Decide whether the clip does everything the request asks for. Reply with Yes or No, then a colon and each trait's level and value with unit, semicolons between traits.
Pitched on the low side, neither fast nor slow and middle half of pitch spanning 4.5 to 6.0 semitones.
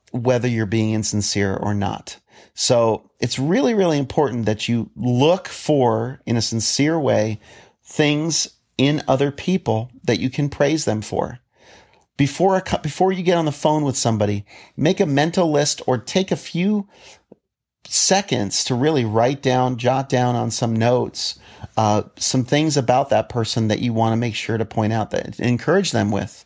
Yes: low, 125 Hz; average, 170 wpm; average, 5.0 semitones